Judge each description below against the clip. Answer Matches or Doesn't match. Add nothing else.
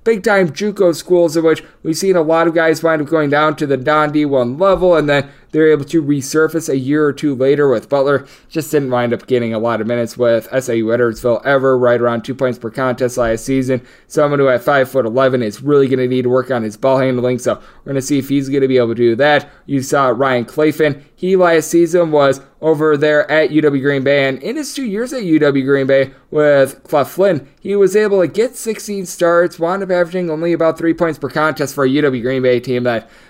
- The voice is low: Doesn't match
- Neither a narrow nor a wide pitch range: Matches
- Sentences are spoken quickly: Matches